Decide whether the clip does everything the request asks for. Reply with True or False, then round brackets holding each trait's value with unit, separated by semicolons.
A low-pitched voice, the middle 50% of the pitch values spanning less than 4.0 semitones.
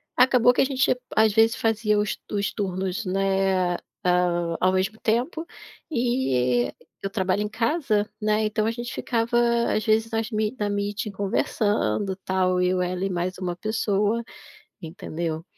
False (210 Hz; 3.1 semitones)